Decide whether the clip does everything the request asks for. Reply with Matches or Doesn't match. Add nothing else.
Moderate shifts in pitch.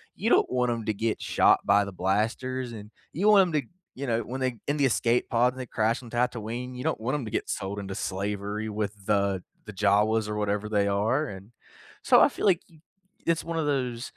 Matches